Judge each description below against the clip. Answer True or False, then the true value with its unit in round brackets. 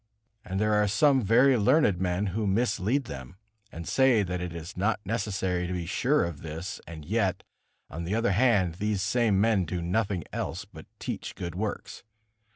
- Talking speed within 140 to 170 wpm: False (180 wpm)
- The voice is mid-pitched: False (100 Hz)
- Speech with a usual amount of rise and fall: True (4.1 semitones)